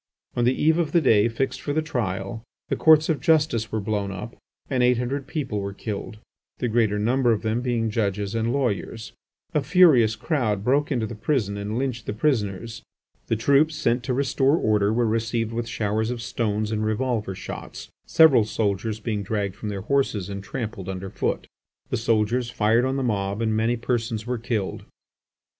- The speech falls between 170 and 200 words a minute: Yes, average, 185 wpm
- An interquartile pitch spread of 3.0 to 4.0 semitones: Yes, average, 3.5 semitones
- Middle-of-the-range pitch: No, low, 115 Hz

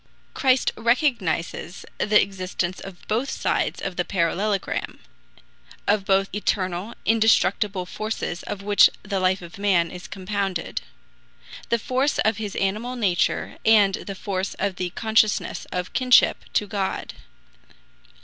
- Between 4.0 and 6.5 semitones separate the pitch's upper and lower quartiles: No, average, 2.8 semitones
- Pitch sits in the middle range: No, high, 200 Hz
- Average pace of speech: No, slow, 130 wpm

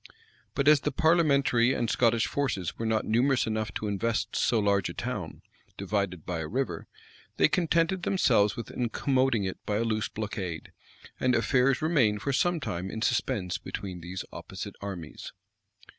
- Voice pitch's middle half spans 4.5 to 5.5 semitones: Yes, average, 5.2 semitones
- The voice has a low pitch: Yes, low, 115 Hz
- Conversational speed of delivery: Yes, average, 160 wpm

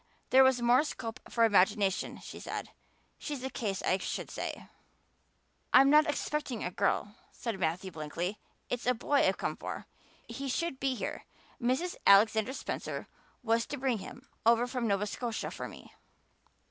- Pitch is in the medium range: No, high, 235 Hz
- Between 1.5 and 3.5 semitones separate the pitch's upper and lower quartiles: No, average, 4.3 semitones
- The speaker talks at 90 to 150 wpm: No, average, 160 wpm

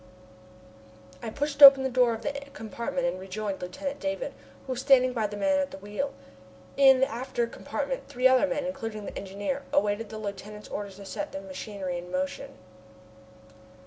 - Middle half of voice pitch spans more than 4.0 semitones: Yes, average, 5.2 semitones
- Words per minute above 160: Yes, average, 175 wpm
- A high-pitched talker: Yes, high, 230 Hz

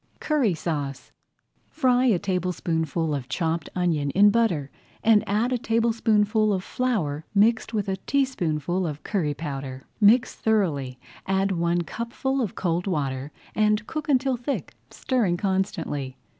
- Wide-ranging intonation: Yes, wide, 6.3 semitones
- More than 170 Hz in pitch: Yes, high, 190 Hz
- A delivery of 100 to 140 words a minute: Yes, slow, 135 wpm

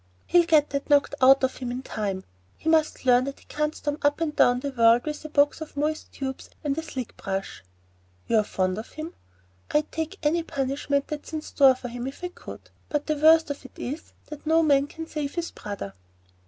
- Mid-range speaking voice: No, very high, 285 Hz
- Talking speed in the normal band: No, fast, 215 wpm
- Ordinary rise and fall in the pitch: Yes, average, 3.3 semitones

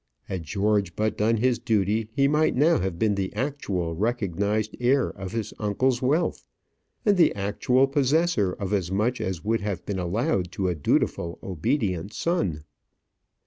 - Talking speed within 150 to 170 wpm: Yes, average, 160 wpm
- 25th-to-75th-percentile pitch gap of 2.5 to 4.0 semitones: No, average, 5.0 semitones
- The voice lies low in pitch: Yes, low, 105 Hz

